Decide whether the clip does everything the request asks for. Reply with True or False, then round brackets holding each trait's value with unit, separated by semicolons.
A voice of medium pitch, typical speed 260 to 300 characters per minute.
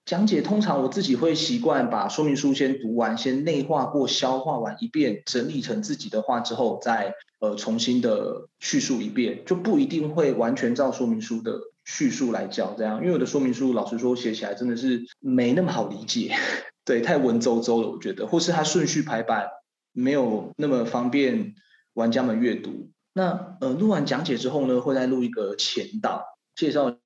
True (145 Hz; 290 characters per minute)